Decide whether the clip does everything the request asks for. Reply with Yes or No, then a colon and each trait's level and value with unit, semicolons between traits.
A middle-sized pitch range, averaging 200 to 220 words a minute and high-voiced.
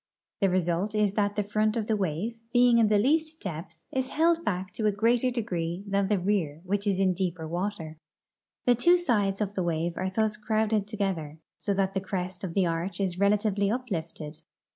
Yes: average, 3.2 semitones; fast, 205 wpm; high, 200 Hz